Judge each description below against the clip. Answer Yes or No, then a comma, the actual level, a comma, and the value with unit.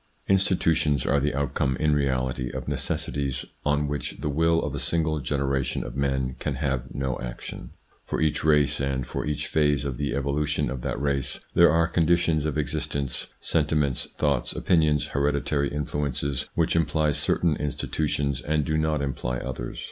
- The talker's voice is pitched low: Yes, very low, 70 Hz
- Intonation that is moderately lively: No, narrow, 2.2 semitones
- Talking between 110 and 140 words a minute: No, average, 165 wpm